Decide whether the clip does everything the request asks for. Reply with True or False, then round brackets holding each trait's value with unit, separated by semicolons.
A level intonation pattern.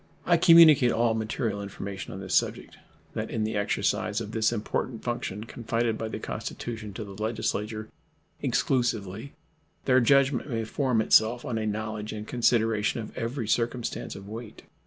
True (2.0 semitones)